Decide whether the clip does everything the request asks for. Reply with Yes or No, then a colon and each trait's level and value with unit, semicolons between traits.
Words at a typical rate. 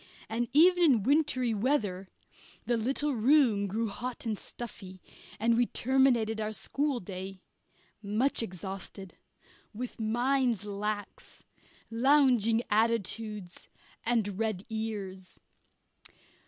No: slow, 100 wpm